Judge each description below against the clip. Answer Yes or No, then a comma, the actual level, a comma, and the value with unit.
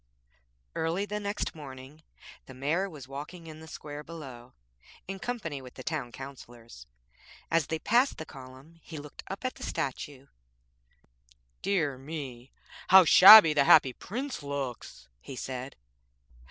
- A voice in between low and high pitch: Yes, medium, 150 Hz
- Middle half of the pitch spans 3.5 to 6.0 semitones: Yes, average, 4.3 semitones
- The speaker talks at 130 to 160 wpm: Yes, average, 140 wpm